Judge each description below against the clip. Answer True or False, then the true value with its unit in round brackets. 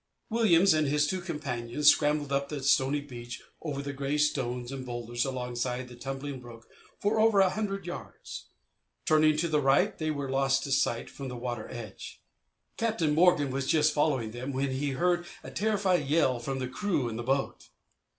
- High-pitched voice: False (140 Hz)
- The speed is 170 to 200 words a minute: True (185 wpm)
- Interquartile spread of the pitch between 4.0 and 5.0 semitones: False (3.6 semitones)